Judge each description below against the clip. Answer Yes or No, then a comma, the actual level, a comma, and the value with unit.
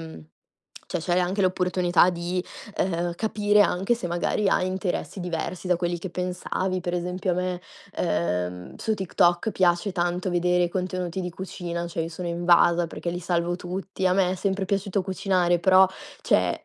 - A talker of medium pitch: Yes, medium, 180 Hz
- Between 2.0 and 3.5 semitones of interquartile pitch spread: No, narrow, 1.4 semitones